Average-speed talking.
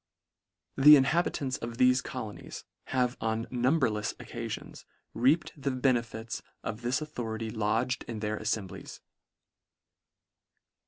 No: slow, 105 wpm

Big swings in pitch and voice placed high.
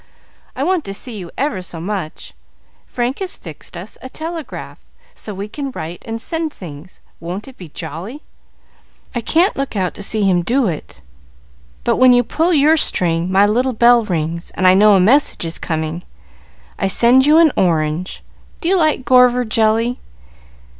Yes: wide, 6.7 semitones; high, 215 Hz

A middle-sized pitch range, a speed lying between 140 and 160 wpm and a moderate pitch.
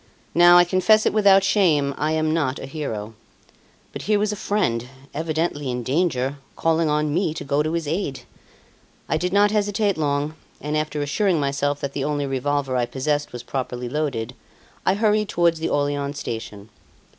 No: average, 4.1 semitones; average, 180 wpm; medium, 150 Hz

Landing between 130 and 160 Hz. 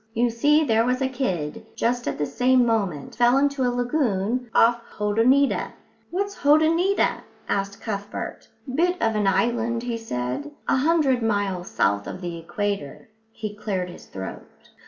No: high, 230 Hz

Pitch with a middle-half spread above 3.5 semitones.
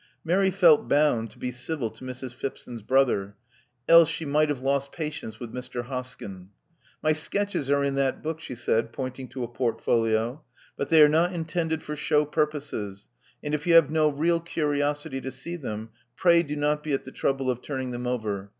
Yes: average, 3.9 semitones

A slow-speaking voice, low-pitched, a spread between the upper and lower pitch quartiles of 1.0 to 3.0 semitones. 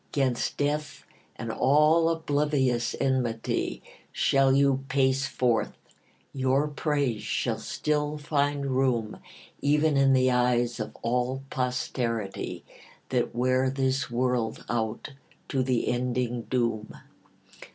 Yes: slow, 110 wpm; low, 130 Hz; narrow, 2.6 semitones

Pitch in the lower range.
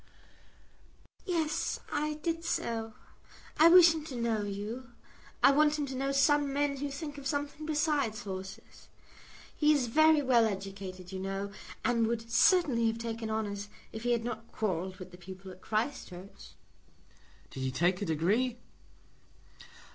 No: high, 230 Hz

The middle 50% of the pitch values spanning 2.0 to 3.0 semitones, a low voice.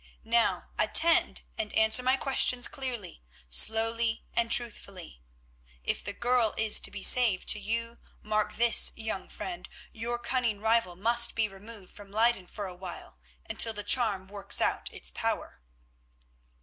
No: narrow, 2.6 semitones; high, 220 Hz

